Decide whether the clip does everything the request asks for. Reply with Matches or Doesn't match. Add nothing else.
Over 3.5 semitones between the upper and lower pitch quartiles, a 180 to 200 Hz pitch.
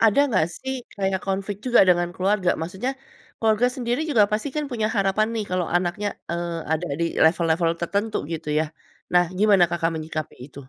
Matches